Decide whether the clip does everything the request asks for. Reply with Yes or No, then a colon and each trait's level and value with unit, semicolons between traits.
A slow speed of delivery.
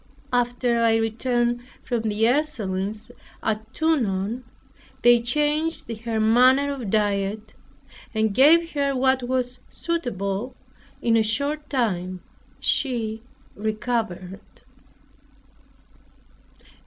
Yes: slow, 95 wpm